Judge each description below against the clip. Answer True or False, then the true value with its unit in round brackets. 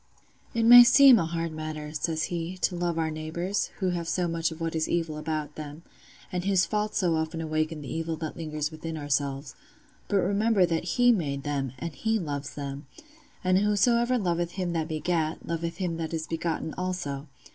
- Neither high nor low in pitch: True (165 Hz)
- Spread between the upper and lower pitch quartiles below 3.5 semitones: True (2.8 semitones)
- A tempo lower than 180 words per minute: False (190 wpm)